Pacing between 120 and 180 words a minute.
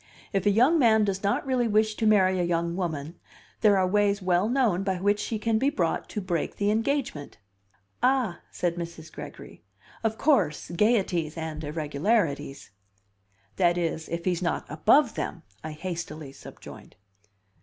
Yes: average, 165 wpm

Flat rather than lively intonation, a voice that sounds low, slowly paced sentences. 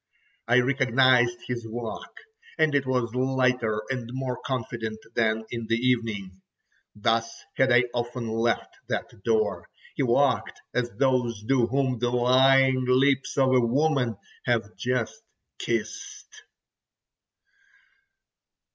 Yes: narrow, 2.3 semitones; low, 125 Hz; slow, 120 wpm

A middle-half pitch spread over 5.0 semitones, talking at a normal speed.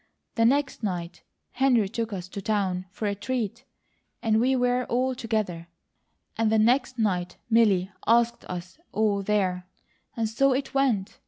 No: average, 4.2 semitones; average, 155 wpm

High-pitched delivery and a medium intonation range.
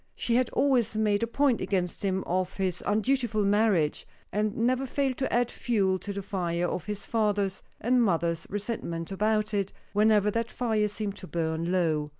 Yes: high, 205 Hz; average, 3.7 semitones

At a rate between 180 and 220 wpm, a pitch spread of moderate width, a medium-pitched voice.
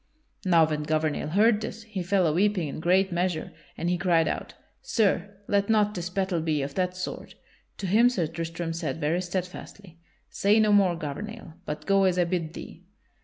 Yes: average, 190 wpm; average, 3.5 semitones; medium, 180 Hz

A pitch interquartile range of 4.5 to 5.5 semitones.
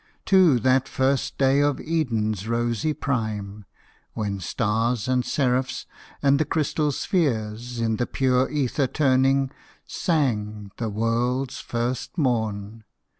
No: average, 3.7 semitones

